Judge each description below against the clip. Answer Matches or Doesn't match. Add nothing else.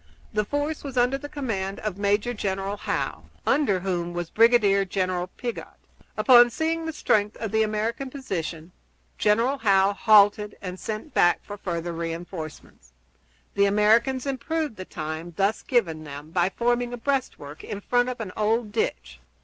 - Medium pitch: Doesn't match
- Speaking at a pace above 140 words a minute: Matches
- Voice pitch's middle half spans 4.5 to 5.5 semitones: Matches